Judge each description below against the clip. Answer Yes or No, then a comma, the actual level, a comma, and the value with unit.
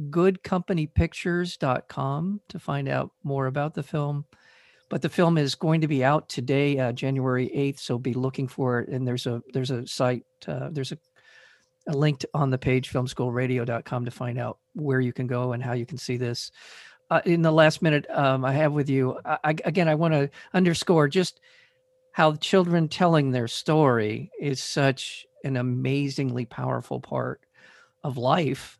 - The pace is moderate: Yes, average, 175 wpm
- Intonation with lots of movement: No, average, 3.9 semitones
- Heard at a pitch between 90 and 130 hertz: No, medium, 140 Hz